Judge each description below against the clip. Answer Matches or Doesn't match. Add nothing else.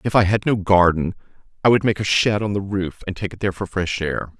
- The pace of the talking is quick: Matches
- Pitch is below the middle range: Matches